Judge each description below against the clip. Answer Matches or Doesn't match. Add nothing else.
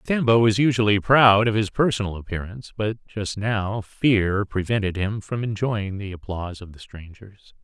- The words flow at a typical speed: Matches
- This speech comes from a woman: Doesn't match